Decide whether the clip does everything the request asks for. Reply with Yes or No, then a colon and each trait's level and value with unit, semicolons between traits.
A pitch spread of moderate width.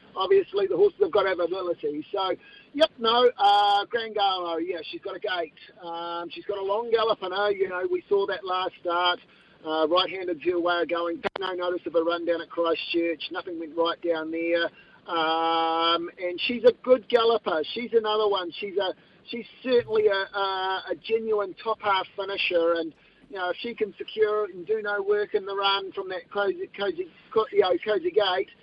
Yes: average, 4.3 semitones